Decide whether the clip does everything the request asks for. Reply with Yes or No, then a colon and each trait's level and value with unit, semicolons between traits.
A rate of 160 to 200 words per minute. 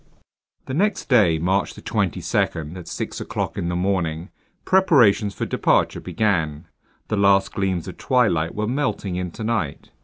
No: average, 145 wpm